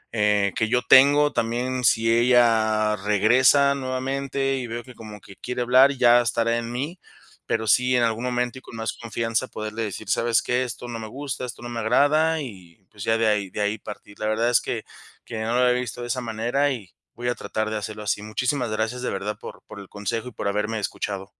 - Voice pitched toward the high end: No, low, 115 Hz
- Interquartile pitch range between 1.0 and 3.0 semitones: Yes, narrow, 2.6 semitones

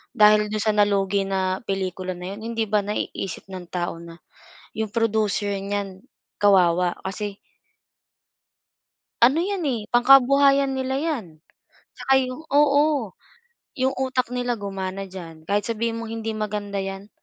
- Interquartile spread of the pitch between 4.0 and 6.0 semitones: Yes, average, 4.4 semitones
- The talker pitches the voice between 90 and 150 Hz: No, high, 210 Hz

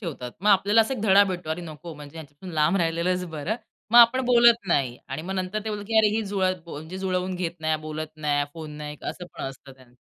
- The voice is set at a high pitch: No, medium, 175 Hz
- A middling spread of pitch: Yes, average, 4.5 semitones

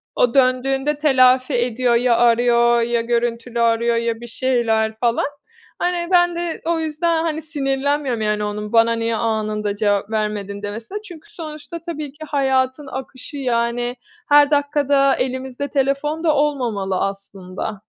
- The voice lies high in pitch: Yes, very high, 250 Hz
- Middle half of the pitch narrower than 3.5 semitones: No, average, 4.1 semitones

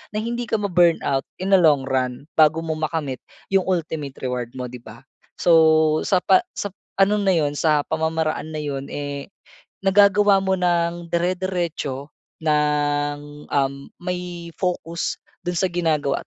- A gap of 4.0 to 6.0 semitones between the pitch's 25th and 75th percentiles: No, average, 3.6 semitones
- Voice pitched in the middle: Yes, medium, 160 Hz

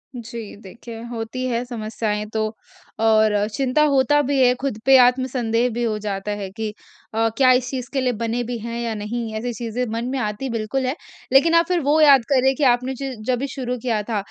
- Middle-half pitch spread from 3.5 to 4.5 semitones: No, average, 2.8 semitones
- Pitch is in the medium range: No, high, 240 Hz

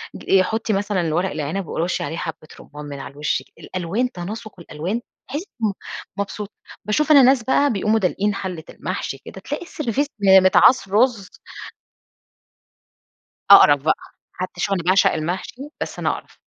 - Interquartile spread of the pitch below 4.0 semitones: No, average, 4.7 semitones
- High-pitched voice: Yes, high, 195 Hz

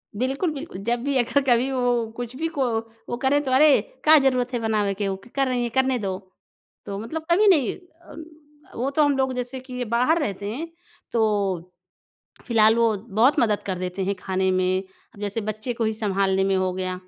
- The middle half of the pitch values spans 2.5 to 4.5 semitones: No, average, 4.9 semitones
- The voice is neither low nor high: No, high, 235 Hz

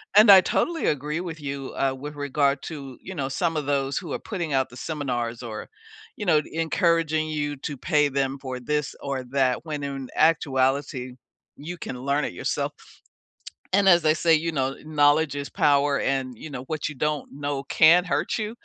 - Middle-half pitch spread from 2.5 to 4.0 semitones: Yes, average, 2.8 semitones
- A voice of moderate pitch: Yes, medium, 145 Hz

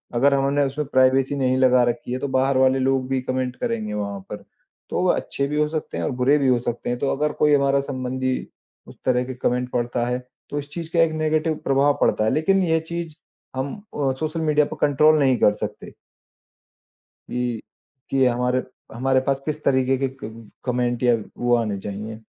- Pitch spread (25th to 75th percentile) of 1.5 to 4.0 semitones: Yes, average, 2.8 semitones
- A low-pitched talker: Yes, low, 130 Hz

